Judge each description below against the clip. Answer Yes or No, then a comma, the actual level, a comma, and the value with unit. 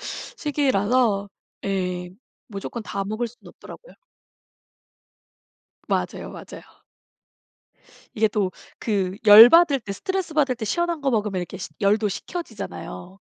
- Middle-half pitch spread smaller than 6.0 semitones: Yes, wide, 5.6 semitones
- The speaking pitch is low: No, high, 215 Hz